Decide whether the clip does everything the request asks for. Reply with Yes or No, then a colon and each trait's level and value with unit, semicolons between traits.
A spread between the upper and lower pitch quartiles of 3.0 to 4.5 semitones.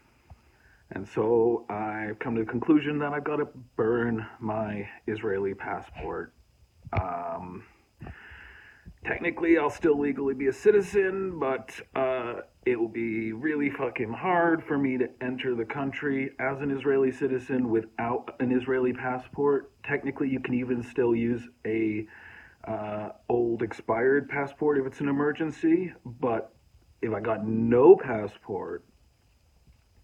Yes: average, 4.2 semitones